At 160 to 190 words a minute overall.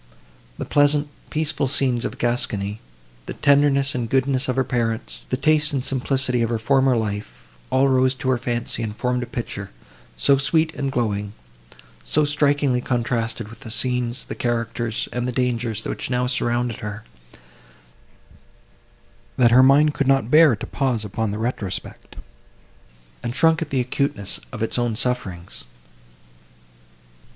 No: average, 145 wpm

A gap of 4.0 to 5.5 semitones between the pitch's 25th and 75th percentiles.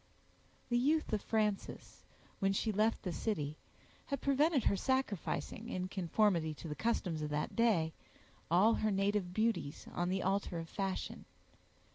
Yes: average, 4.5 semitones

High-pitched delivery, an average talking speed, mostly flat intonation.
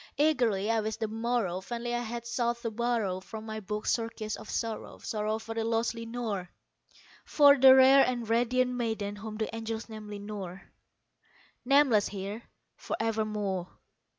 Yes: high, 225 Hz; average, 155 wpm; narrow, 2.1 semitones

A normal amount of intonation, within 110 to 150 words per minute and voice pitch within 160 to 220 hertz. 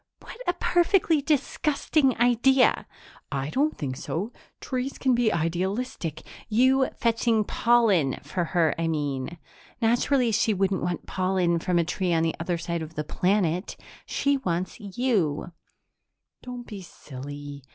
No: wide, 7.0 semitones; average, 140 wpm; high, 190 Hz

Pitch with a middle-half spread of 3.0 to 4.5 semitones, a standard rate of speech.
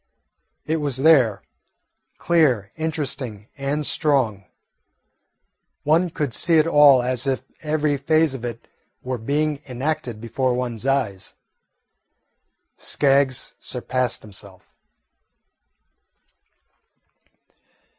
No: average, 3.9 semitones; slow, 90 wpm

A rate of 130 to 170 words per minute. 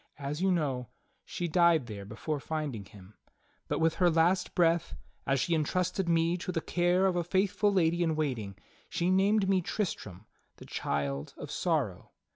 No: average, 180 wpm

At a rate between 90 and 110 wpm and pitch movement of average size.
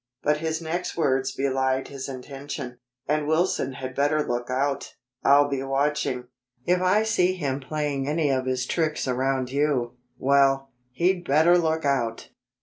No: average, 145 wpm; average, 3.1 semitones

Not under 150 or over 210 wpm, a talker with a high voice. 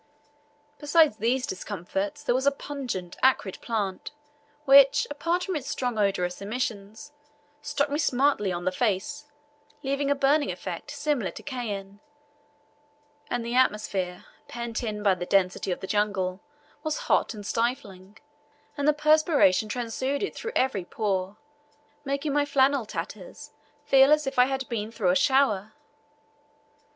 No: average, 140 wpm; high, 240 Hz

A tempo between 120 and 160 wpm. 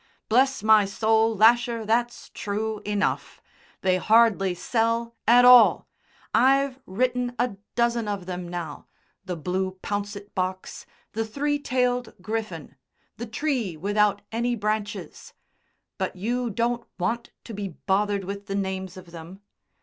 Yes: slow, 135 wpm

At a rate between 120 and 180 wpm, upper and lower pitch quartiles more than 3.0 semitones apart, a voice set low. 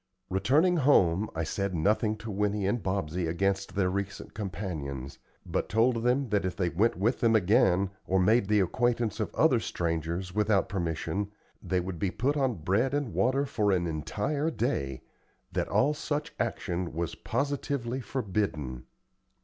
Yes: average, 155 wpm; average, 4.9 semitones; low, 100 Hz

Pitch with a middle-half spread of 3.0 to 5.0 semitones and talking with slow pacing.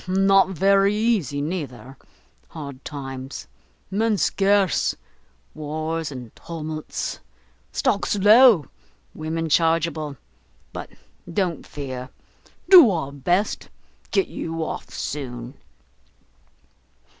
No: wide, 5.5 semitones; slow, 85 wpm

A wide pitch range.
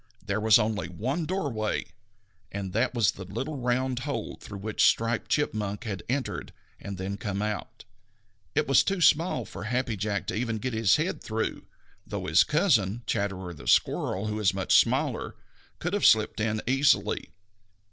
No: average, 4.3 semitones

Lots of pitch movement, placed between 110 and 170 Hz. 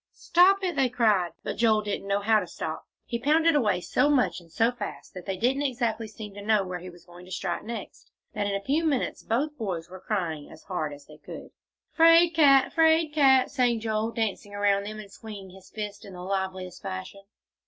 No: wide, 5.7 semitones; high, 215 Hz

